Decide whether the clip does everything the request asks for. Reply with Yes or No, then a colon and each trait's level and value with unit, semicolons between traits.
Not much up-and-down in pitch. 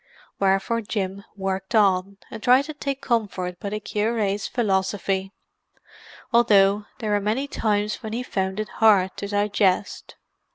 Yes: narrow, 2.3 semitones